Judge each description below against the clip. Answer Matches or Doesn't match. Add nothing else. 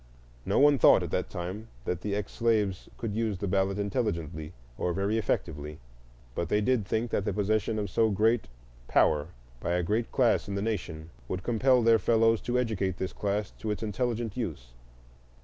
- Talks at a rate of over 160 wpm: Matches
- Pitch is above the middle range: Doesn't match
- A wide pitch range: Doesn't match